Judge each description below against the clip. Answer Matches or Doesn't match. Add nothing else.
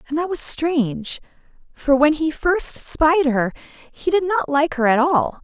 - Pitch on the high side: Matches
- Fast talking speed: Doesn't match